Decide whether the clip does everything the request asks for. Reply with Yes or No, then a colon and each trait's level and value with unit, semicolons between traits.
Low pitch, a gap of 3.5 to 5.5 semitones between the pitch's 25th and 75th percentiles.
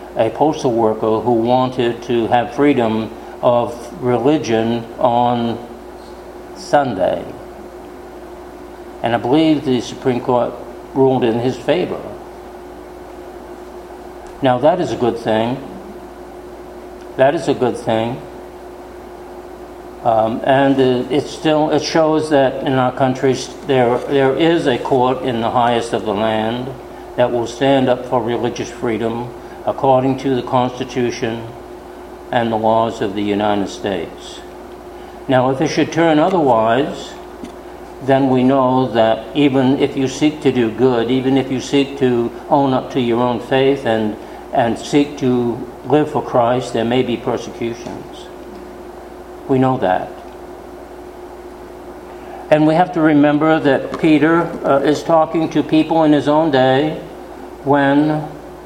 Yes: low, 130 Hz; average, 3.8 semitones